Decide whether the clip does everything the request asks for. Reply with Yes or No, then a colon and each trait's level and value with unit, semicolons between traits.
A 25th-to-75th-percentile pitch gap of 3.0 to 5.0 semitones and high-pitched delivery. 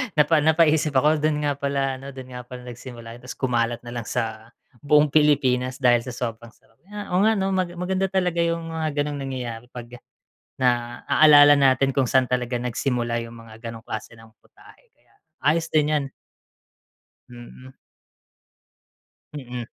No: average, 4.0 semitones; low, 130 Hz